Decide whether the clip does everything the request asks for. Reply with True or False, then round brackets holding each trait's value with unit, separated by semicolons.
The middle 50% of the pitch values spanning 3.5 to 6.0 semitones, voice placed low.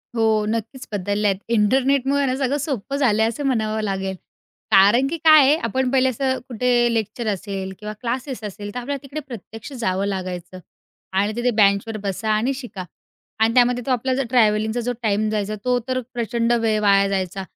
False (3.8 semitones; 225 Hz)